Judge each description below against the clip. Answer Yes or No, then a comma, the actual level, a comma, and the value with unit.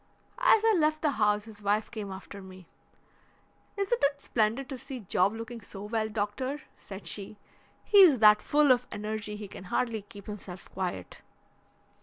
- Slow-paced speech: No, average, 165 wpm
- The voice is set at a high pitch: Yes, high, 215 Hz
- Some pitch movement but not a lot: Yes, average, 4.3 semitones